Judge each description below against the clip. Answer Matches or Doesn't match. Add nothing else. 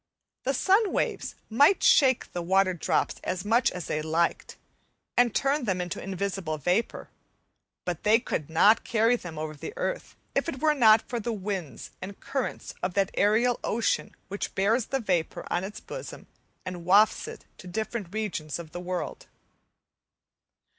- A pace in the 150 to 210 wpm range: Matches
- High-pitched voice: Matches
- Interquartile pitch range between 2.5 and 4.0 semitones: Doesn't match